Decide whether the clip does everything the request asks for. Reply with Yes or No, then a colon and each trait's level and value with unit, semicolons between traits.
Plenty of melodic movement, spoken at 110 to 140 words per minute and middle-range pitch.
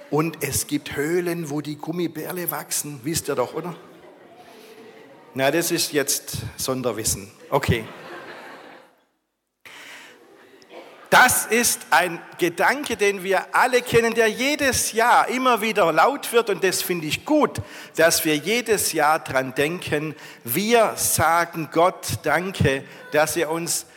Yes: wide, 6.6 semitones; average, 130 wpm; medium, 170 Hz